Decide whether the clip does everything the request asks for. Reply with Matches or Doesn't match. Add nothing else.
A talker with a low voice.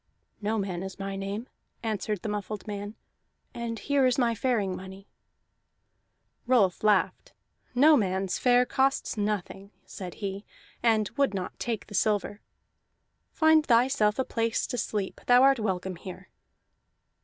Doesn't match